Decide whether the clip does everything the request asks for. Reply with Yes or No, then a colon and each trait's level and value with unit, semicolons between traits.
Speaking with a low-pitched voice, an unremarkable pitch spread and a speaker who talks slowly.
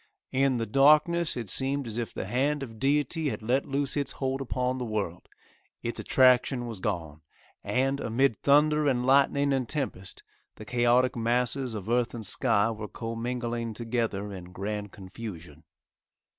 No: low, 120 Hz; average, 4.0 semitones; average, 155 wpm